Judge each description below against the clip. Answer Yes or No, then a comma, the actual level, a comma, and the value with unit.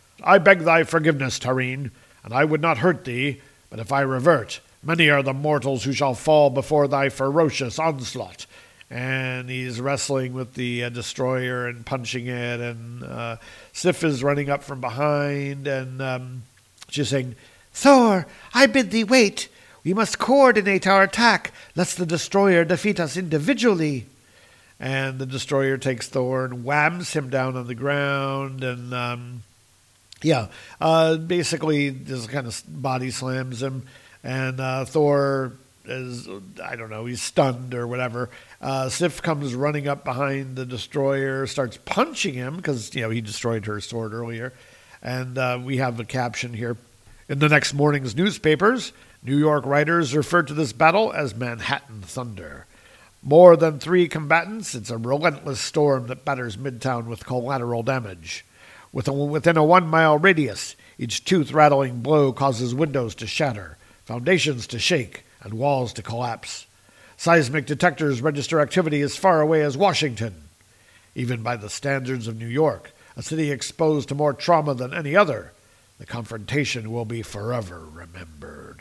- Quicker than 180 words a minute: No, average, 155 wpm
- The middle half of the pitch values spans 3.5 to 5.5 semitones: Yes, average, 3.9 semitones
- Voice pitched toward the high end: No, low, 135 Hz